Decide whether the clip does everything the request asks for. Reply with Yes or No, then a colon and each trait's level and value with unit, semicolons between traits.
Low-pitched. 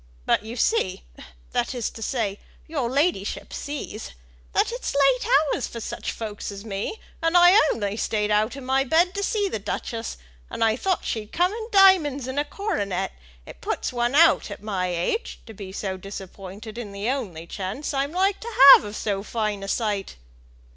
No: high, 230 Hz